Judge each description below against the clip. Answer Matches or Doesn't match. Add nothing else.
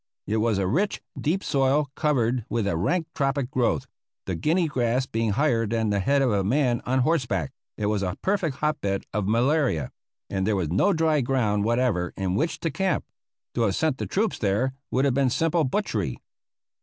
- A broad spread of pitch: Matches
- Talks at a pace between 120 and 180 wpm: Doesn't match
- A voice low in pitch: Matches